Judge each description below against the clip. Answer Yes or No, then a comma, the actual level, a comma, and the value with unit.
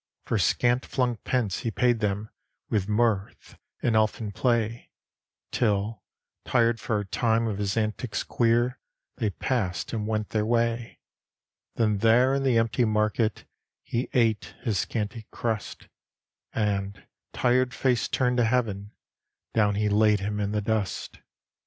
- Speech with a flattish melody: Yes, narrow, 2.3 semitones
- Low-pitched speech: Yes, low, 110 Hz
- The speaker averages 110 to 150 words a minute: Yes, average, 140 wpm